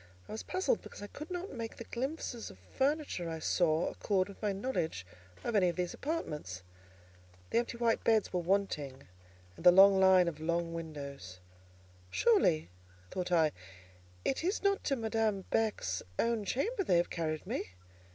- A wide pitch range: Yes, wide, 6.4 semitones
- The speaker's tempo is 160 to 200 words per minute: Yes, average, 170 wpm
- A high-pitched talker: Yes, high, 195 Hz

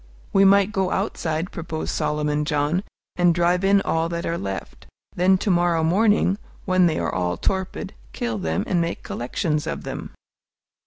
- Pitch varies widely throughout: No, average, 3.9 semitones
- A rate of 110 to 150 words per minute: No, average, 165 wpm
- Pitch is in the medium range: Yes, medium, 170 Hz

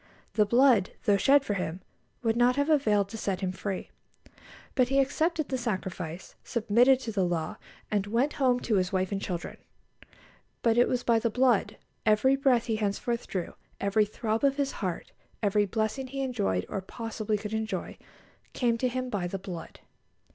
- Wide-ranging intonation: No, average, 4.3 semitones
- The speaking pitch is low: No, high, 220 Hz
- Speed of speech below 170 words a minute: No, average, 180 wpm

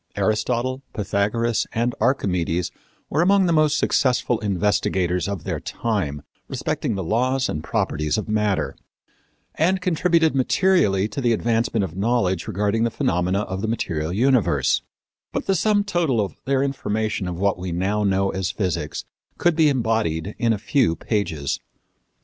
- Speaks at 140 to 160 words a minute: Yes, average, 150 wpm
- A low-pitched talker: Yes, low, 110 Hz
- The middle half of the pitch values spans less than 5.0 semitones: No, wide, 5.6 semitones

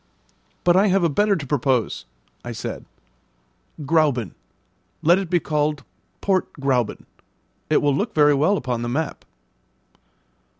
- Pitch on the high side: No, medium, 150 Hz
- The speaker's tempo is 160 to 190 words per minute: No, slow, 135 wpm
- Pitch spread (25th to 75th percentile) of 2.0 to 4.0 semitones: No, average, 4.6 semitones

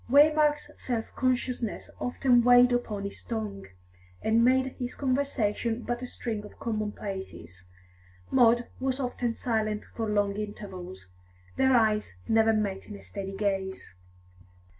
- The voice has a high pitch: Yes, high, 225 Hz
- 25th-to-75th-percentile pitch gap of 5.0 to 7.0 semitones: No, average, 3.3 semitones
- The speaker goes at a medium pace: No, slow, 130 wpm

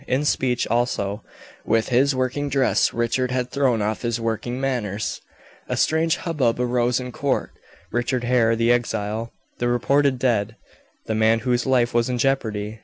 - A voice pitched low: Yes, low, 120 Hz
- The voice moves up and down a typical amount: No, narrow, 2.2 semitones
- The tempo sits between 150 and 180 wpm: Yes, average, 160 wpm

